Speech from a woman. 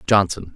No: male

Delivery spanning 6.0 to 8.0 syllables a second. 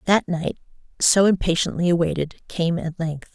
No: 4.9 syllables/s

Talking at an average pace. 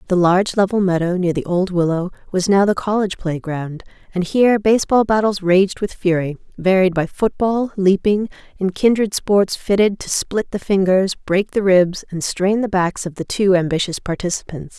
Yes: average, 180 wpm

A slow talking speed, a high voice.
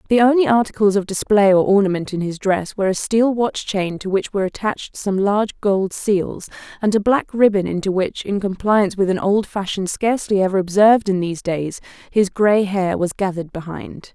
No: average, 200 wpm; high, 200 Hz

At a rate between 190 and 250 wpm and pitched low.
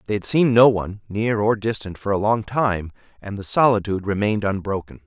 Yes: average, 200 wpm; low, 105 Hz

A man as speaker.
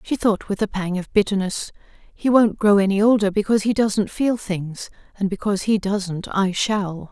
No: female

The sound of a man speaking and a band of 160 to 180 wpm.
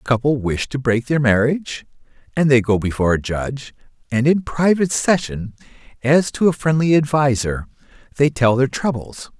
Yes: male; average, 165 wpm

